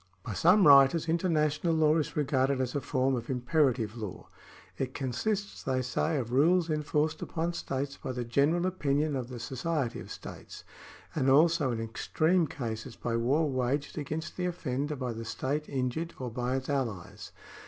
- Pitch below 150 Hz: Yes, medium, 140 Hz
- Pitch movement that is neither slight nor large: Yes, average, 3.9 semitones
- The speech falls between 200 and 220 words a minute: No, average, 170 wpm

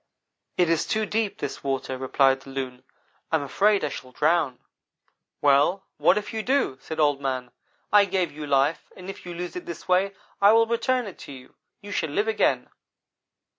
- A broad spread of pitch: Yes, wide, 6.7 semitones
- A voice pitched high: No, medium, 165 Hz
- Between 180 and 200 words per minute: Yes, average, 195 wpm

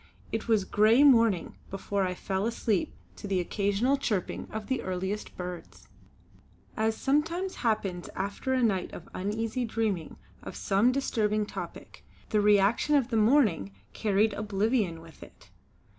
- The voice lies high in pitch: Yes, high, 210 Hz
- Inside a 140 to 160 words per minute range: Yes, average, 145 wpm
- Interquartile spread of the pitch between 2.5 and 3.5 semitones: Yes, average, 3.1 semitones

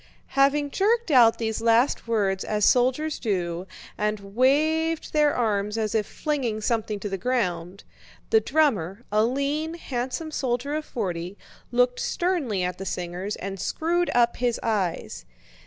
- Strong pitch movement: Yes, wide, 6.1 semitones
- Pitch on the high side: Yes, high, 235 Hz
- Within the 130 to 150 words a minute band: Yes, average, 140 wpm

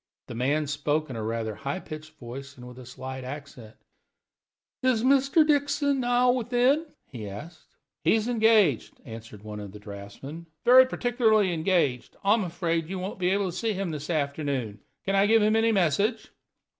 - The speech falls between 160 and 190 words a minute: Yes, average, 180 wpm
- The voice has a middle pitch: Yes, medium, 165 Hz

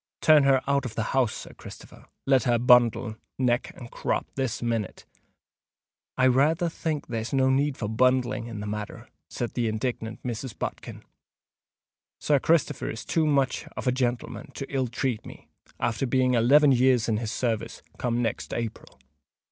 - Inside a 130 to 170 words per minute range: Yes, average, 165 wpm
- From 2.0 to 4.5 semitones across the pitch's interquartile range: Yes, narrow, 2.6 semitones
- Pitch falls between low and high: No, low, 125 Hz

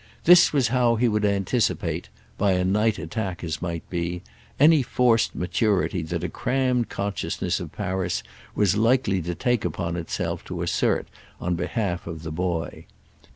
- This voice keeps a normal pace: Yes, average, 150 wpm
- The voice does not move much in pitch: No, average, 5.1 semitones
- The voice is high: No, very low, 95 Hz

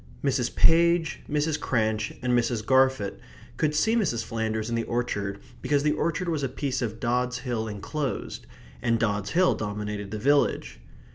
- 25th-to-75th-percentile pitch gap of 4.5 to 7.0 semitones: Yes, average, 5.0 semitones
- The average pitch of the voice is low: Yes, low, 120 Hz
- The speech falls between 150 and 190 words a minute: Yes, average, 160 wpm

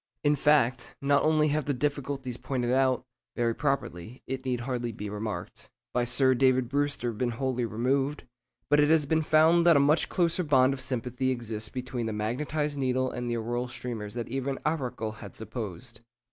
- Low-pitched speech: Yes, low, 130 Hz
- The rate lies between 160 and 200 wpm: Yes, average, 180 wpm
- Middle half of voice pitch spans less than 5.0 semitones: Yes, average, 3.2 semitones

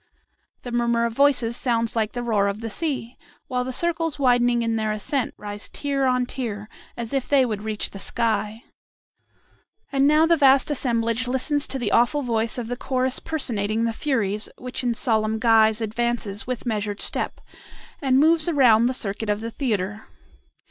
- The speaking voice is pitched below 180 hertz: No, high, 235 Hz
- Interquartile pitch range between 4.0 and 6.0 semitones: No, average, 3.2 semitones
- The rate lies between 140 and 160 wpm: No, average, 175 wpm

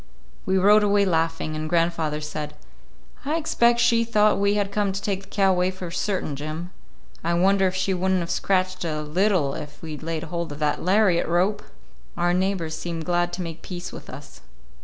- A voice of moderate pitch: Yes, medium, 180 Hz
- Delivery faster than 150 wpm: Yes, average, 200 wpm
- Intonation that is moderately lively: Yes, average, 3.3 semitones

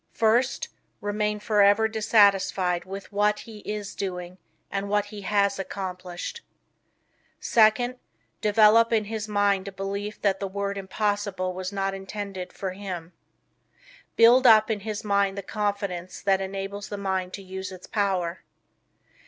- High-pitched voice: Yes, high, 200 Hz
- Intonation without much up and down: Yes, narrow, 1.7 semitones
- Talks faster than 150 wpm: No, average, 145 wpm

